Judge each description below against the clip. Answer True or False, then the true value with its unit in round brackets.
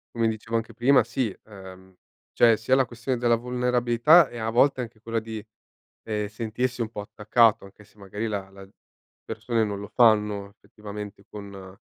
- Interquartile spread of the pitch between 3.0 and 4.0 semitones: False (2.6 semitones)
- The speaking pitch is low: True (110 Hz)